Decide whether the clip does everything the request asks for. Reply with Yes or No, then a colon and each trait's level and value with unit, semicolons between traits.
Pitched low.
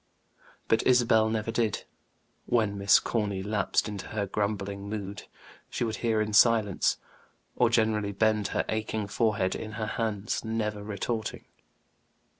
Yes: low, 110 Hz